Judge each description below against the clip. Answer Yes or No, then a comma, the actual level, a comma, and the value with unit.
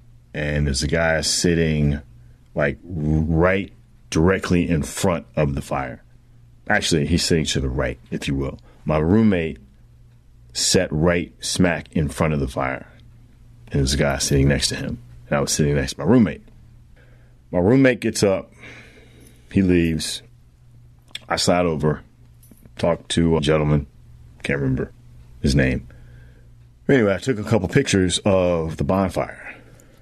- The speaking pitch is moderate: No, very low, 75 Hz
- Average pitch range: No, wide, 5.8 semitones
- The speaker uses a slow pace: No, average, 150 wpm